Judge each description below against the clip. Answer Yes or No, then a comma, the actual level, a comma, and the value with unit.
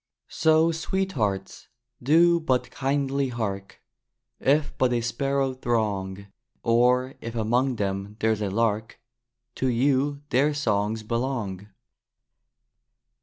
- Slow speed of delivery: Yes, slow, 105 wpm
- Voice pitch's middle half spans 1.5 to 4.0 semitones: No, average, 4.5 semitones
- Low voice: Yes, low, 120 Hz